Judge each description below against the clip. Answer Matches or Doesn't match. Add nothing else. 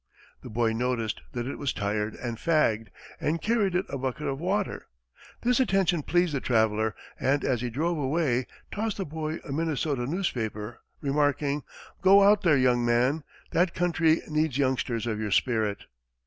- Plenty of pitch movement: Matches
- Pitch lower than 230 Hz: Matches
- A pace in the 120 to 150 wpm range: Doesn't match